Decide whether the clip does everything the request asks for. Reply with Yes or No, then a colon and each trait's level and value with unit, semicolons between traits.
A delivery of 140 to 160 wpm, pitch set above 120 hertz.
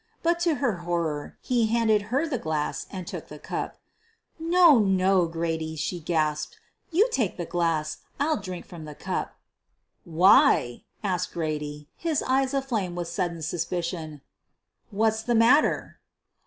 Yes: average, 145 wpm; medium, 185 Hz